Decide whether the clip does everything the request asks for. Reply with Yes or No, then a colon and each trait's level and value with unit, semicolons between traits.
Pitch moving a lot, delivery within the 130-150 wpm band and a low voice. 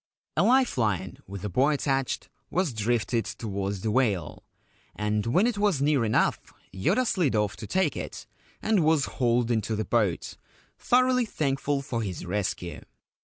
No: wide, 6.6 semitones; average, 160 wpm; low, 120 Hz